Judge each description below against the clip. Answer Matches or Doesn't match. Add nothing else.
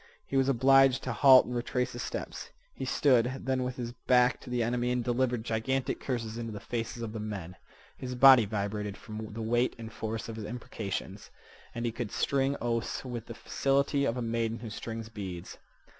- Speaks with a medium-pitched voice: Doesn't match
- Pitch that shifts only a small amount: Matches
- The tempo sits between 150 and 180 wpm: Doesn't match